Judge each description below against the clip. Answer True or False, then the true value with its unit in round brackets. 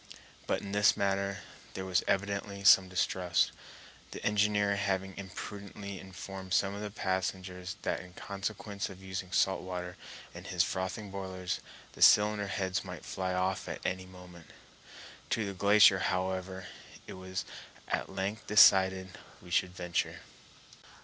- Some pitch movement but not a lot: False (1.3 semitones)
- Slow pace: False (145 wpm)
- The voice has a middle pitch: False (95 Hz)